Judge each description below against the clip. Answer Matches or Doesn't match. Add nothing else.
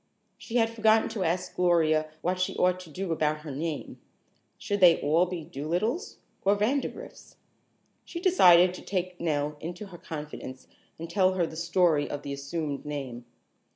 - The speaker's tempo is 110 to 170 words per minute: Matches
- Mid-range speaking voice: Matches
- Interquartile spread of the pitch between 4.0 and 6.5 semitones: Doesn't match